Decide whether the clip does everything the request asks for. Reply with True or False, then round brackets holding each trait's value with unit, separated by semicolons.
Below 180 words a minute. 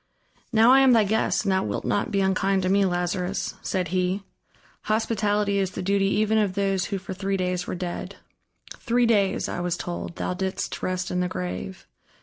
False (195 wpm)